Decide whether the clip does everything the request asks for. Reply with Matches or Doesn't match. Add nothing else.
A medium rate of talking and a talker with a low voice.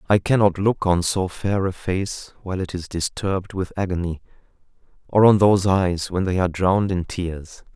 Matches